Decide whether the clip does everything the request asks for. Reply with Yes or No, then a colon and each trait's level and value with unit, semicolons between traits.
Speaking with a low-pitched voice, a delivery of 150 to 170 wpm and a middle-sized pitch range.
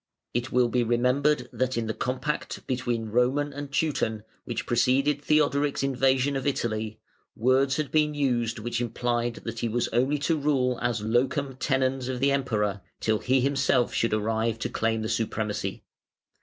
Yes: low, 125 Hz; average, 165 wpm; average, 3.2 semitones